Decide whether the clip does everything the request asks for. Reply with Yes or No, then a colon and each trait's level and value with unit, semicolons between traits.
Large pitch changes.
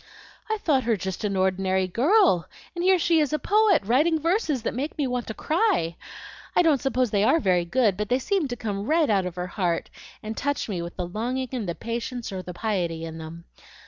Yes: wide, 8.1 semitones